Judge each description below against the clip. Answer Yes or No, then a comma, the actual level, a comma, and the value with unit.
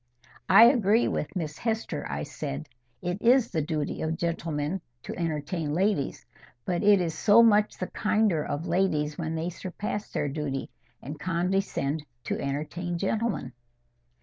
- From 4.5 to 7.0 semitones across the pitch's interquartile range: Yes, average, 5.1 semitones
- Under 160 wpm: Yes, average, 150 wpm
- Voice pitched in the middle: Yes, medium, 170 Hz